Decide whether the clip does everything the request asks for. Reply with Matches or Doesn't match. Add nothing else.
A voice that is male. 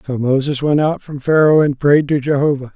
Matches